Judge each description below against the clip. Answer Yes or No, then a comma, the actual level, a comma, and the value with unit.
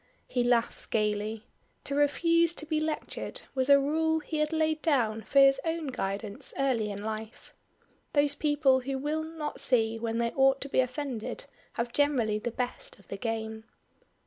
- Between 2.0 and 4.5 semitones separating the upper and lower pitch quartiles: No, average, 5.0 semitones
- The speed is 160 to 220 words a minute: Yes, average, 170 wpm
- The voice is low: No, very high, 265 Hz